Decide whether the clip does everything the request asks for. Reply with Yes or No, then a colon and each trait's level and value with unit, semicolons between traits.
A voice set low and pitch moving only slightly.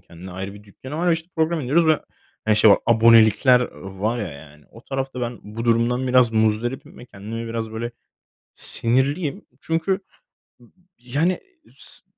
No: low, 115 Hz; average, 3.9 semitones